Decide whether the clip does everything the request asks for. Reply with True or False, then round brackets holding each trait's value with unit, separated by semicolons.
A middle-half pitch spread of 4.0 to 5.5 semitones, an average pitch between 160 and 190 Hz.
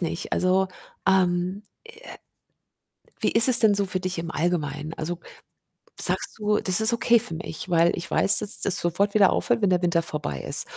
False (3.3 semitones; 185 Hz)